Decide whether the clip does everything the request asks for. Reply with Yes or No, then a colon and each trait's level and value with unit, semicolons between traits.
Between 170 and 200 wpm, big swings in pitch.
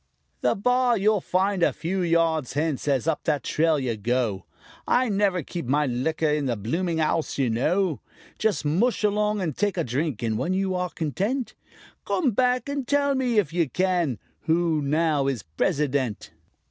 Yes: average, 175 wpm; wide, 6.1 semitones